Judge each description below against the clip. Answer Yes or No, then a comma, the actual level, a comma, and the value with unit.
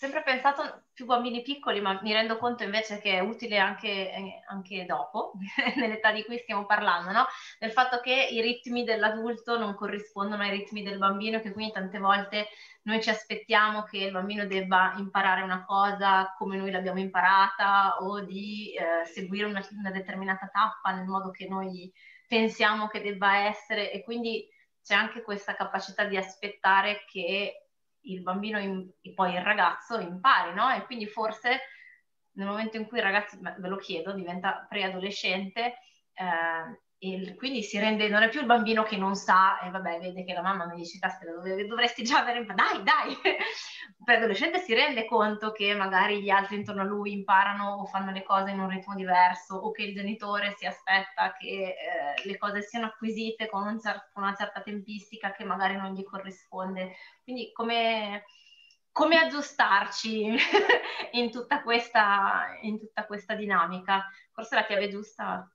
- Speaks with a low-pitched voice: No, high, 205 Hz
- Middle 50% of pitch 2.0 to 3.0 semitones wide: Yes, narrow, 2.5 semitones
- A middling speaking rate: No, fast, 175 wpm